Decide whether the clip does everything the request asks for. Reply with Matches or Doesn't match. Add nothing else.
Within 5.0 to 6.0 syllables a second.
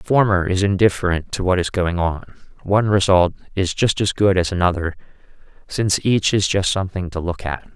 Matches